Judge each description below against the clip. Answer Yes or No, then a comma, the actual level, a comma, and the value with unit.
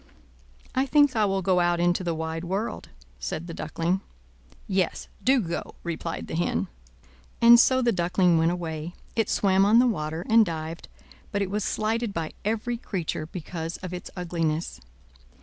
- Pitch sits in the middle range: Yes, medium, 180 Hz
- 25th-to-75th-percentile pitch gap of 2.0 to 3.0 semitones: No, average, 4.5 semitones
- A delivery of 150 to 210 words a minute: Yes, average, 165 wpm